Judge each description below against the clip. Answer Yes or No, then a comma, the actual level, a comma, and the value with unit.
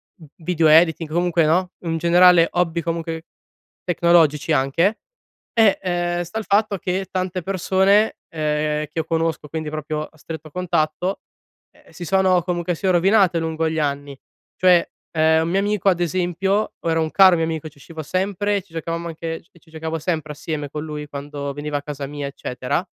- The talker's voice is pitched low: No, medium, 165 Hz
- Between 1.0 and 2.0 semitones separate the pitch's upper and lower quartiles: No, average, 2.7 semitones